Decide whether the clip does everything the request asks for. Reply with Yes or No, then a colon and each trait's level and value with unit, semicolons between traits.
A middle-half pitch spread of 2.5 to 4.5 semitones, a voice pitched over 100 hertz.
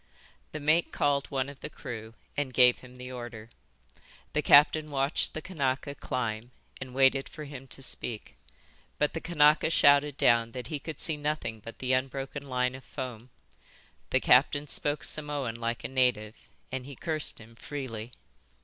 Yes: average, 2.9 semitones; low, 135 Hz